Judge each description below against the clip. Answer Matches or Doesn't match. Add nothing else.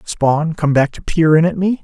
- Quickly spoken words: Matches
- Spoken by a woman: Doesn't match